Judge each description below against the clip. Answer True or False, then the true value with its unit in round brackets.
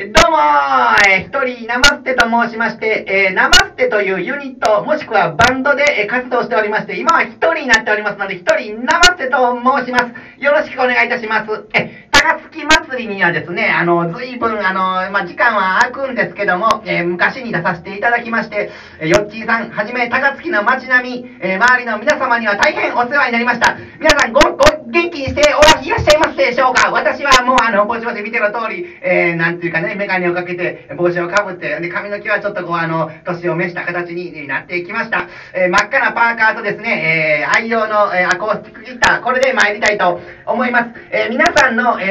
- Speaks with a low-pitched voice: False (230 Hz)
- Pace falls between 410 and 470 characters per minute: True (435 characters per minute)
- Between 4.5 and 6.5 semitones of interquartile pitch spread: True (5.1 semitones)